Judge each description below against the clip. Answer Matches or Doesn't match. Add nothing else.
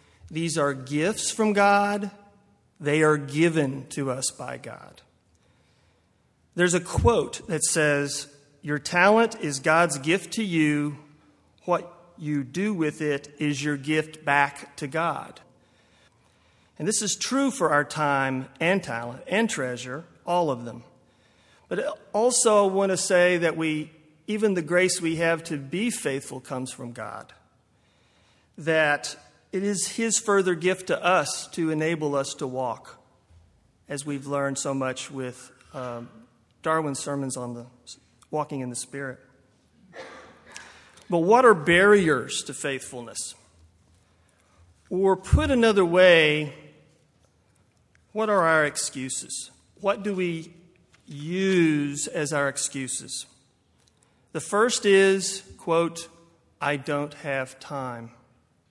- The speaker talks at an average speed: Doesn't match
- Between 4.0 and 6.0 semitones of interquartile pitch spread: Matches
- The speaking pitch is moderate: Matches